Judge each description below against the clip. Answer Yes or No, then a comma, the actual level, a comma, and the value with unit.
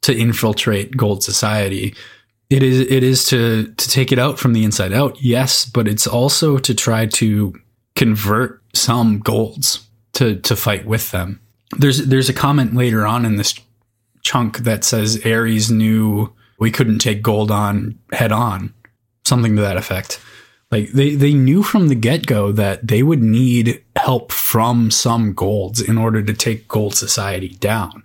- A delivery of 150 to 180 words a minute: Yes, average, 165 wpm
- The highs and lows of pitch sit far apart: No, average, 2.8 semitones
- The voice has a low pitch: Yes, low, 115 Hz